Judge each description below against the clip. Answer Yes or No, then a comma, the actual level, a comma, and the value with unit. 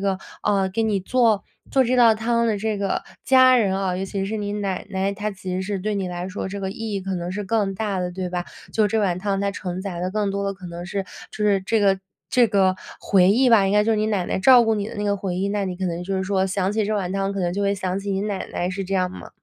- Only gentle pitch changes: Yes, narrow, 1.9 semitones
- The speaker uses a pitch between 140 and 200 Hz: Yes, high, 195 Hz